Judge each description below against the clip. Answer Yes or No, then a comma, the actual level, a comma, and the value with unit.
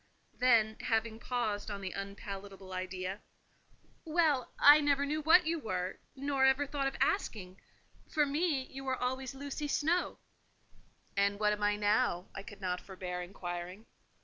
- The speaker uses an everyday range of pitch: No, wide, 6.4 semitones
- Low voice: No, high, 220 Hz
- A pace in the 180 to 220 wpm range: No, average, 150 wpm